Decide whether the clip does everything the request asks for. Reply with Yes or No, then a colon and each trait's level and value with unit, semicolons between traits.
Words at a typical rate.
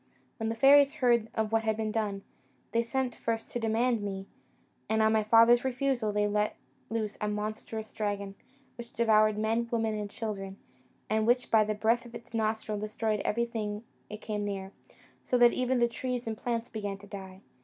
Yes: average, 185 wpm